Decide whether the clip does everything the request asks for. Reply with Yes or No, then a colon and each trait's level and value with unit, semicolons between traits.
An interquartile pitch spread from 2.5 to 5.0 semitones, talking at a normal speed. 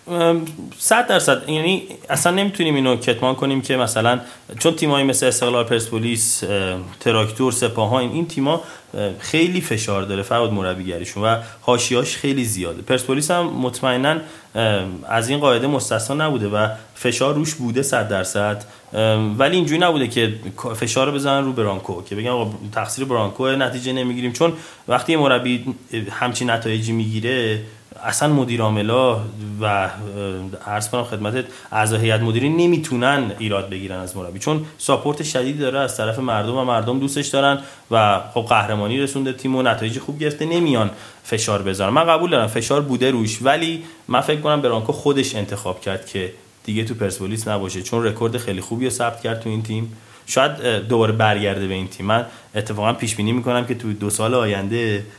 No: average, 3.9 semitones; fast, 160 wpm